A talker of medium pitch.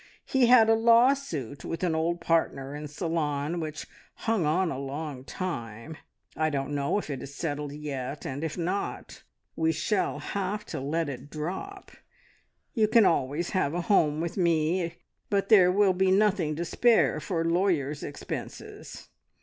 Yes: medium, 165 Hz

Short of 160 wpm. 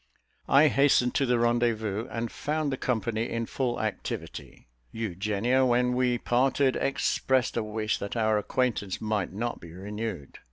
Yes: average, 150 wpm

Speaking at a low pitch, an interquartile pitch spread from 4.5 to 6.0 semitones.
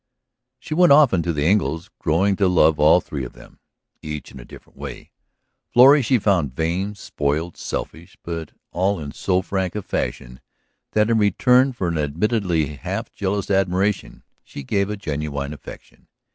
Yes: very low, 90 Hz; average, 5.2 semitones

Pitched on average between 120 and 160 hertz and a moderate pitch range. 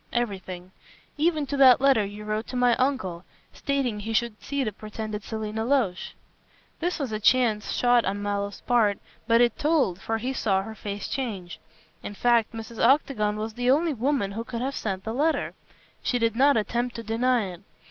No: high, 230 Hz; average, 3.4 semitones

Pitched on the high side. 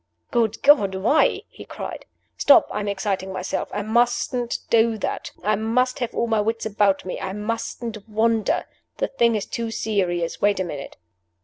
Yes: high, 220 Hz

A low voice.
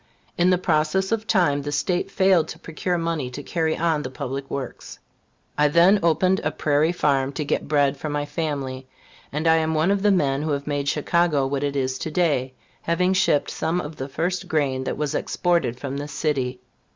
No: medium, 150 Hz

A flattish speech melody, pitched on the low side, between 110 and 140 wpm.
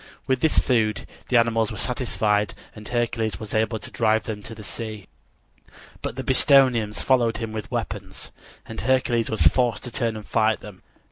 No: narrow, 2.1 semitones; low, 115 Hz; average, 180 wpm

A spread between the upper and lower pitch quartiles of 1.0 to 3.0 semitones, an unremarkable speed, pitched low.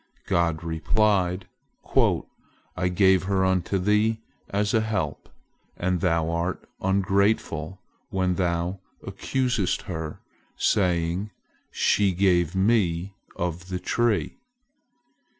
No: narrow, 2.5 semitones; slow, 95 wpm; very low, 95 Hz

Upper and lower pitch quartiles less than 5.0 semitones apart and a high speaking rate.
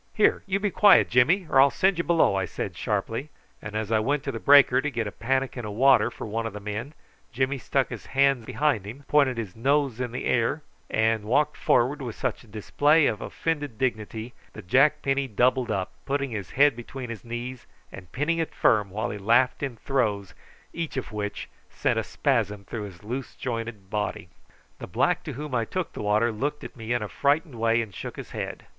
Yes: average, 4.4 semitones; fast, 215 wpm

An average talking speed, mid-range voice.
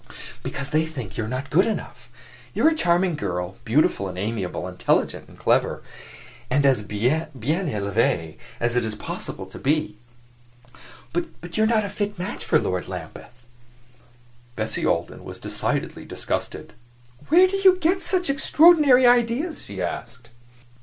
Yes: average, 155 wpm; medium, 145 Hz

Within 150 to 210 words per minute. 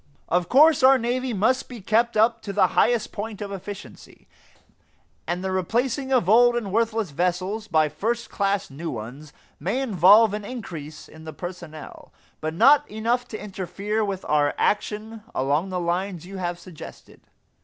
Yes: average, 165 wpm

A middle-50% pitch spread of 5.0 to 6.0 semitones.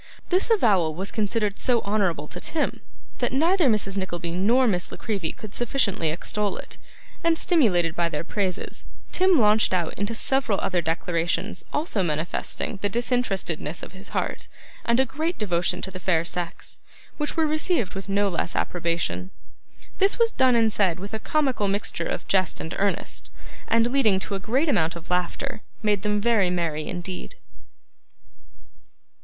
Yes: wide, 5.4 semitones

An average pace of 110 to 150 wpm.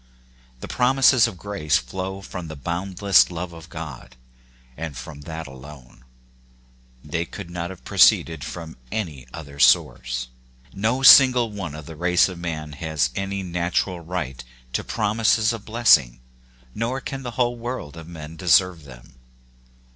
Yes: average, 145 wpm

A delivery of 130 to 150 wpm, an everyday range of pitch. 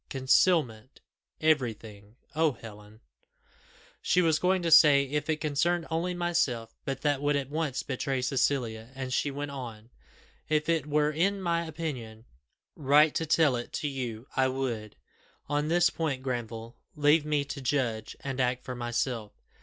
No: average, 160 wpm; average, 4.2 semitones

